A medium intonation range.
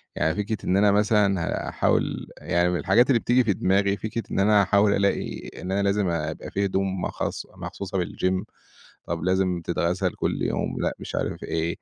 No: narrow, 2.3 semitones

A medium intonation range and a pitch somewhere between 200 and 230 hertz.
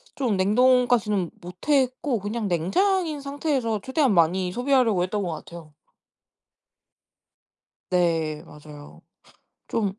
No: wide, 6.6 semitones; high, 210 Hz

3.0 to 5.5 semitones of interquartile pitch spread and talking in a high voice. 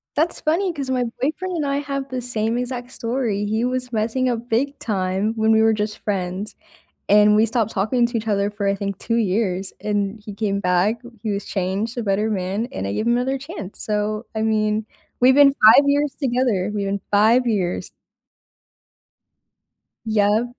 Yes: average, 3.5 semitones; high, 220 Hz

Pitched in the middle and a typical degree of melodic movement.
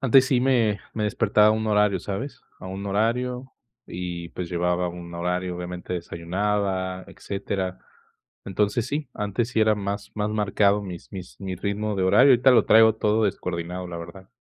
No: low, 100 Hz; average, 3.1 semitones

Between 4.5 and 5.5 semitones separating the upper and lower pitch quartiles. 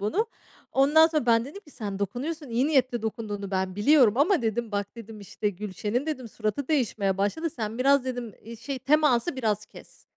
Yes: average, 5.2 semitones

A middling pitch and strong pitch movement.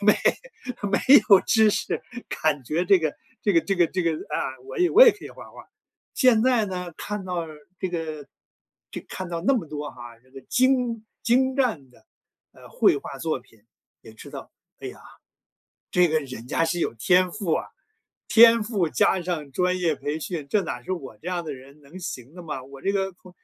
Yes: medium, 175 Hz; wide, 5.7 semitones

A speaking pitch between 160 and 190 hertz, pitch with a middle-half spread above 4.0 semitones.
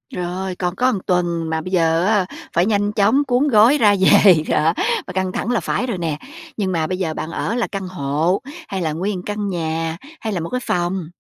No: medium, 185 Hz; average, 3.7 semitones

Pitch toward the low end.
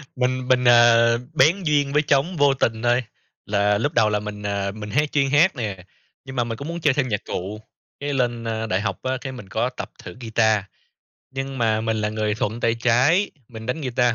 Yes: low, 120 Hz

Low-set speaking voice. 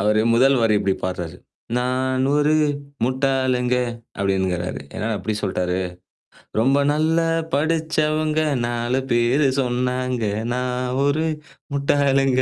Yes: low, 125 Hz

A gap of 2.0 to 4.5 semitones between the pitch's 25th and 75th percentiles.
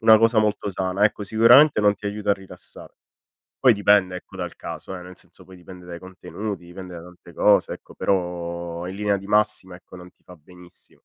Yes: narrow, 2.6 semitones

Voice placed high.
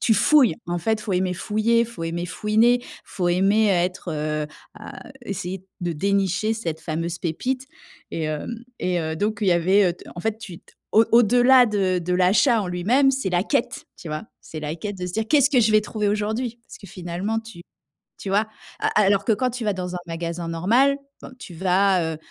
Yes: high, 195 Hz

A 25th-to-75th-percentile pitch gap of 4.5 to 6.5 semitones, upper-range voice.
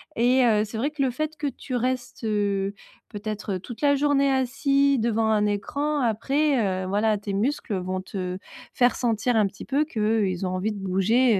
Yes: average, 4.8 semitones; high, 225 Hz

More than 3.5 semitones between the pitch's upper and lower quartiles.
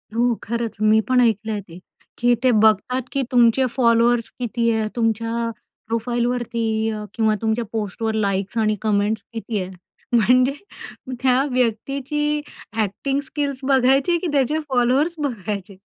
No: average, 2.7 semitones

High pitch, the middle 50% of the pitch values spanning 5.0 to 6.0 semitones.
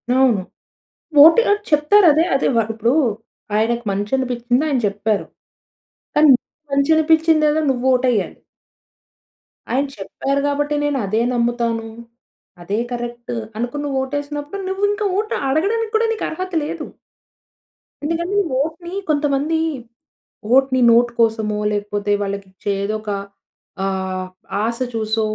Yes: very high, 265 Hz; wide, 5.6 semitones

